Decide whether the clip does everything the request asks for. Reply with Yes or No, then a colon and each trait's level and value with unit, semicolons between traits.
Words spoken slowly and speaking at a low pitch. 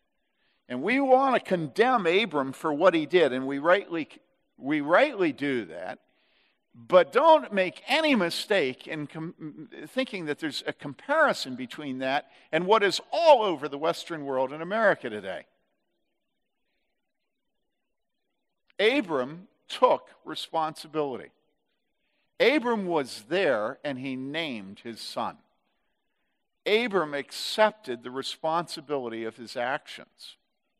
No: slow, 115 wpm; medium, 165 Hz